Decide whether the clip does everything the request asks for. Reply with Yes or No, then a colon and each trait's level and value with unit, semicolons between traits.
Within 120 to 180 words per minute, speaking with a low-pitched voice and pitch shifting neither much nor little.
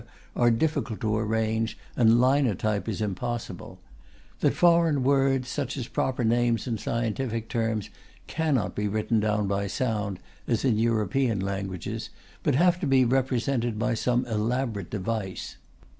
Yes: average, 140 wpm; low, 115 Hz; average, 3.2 semitones